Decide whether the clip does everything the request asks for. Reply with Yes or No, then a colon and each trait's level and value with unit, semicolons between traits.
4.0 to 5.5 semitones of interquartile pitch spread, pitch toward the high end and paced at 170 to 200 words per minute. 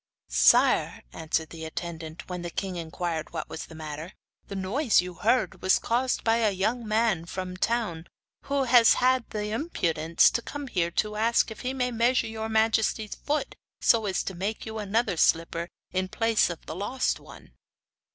Yes: average, 5.2 semitones; high, 210 Hz; average, 180 wpm